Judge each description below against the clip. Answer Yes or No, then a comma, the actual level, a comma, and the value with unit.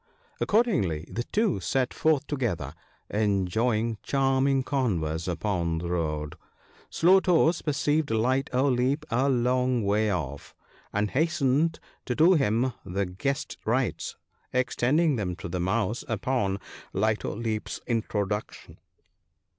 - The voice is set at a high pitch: No, low, 120 Hz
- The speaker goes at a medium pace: No, slow, 125 wpm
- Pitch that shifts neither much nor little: No, wide, 5.8 semitones